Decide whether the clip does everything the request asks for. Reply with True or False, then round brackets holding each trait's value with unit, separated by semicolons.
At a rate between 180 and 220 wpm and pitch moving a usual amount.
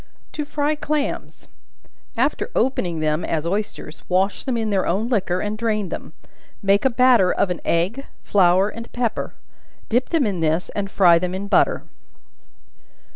False (160 wpm; 4.7 semitones)